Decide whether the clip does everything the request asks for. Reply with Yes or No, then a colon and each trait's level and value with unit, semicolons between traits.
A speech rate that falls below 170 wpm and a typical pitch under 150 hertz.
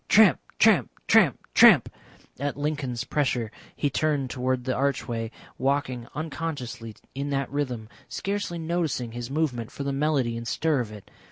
Yes: average, 150 wpm; low, 135 Hz